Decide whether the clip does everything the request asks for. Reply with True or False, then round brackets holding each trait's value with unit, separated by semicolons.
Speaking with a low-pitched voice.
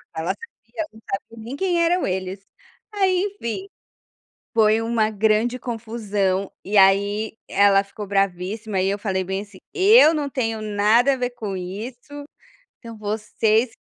False (220 Hz)